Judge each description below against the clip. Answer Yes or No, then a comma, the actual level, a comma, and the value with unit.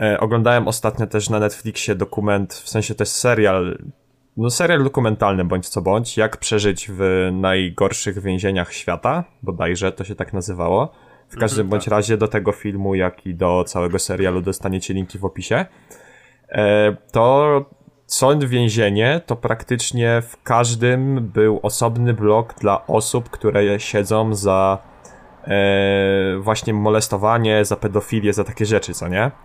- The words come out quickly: No, average, 140 wpm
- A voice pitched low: Yes, low, 105 Hz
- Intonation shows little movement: No, average, 3.2 semitones